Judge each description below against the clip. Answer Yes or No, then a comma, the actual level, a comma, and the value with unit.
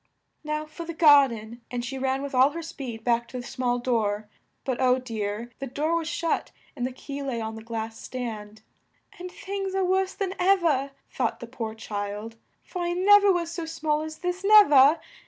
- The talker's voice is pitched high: Yes, very high, 270 Hz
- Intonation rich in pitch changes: Yes, wide, 6.2 semitones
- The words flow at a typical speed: No, fast, 210 wpm